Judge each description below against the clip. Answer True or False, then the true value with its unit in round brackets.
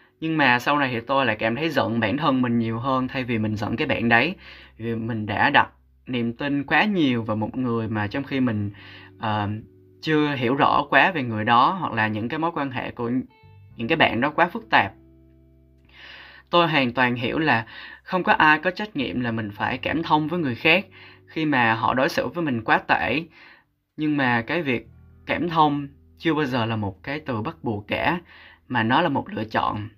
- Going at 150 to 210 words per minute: False (220 wpm)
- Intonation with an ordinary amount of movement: True (5.0 semitones)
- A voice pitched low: True (120 Hz)